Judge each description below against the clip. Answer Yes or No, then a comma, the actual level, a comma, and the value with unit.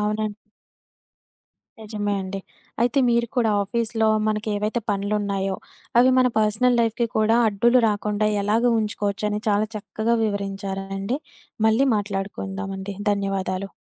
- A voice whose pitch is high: Yes, high, 210 Hz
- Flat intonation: Yes, narrow, 1.9 semitones